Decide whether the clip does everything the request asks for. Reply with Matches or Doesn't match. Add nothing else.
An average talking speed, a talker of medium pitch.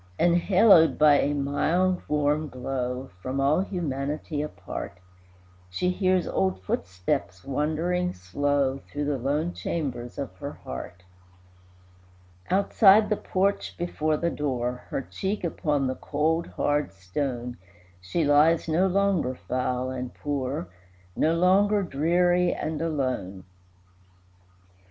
Doesn't match